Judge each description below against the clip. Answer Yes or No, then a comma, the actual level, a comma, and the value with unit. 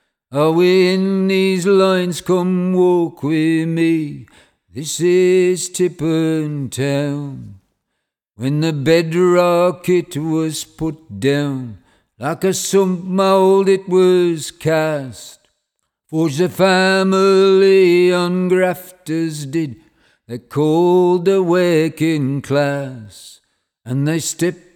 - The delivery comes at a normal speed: No, slow, 100 wpm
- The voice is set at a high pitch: No, medium, 165 Hz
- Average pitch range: Yes, average, 3.7 semitones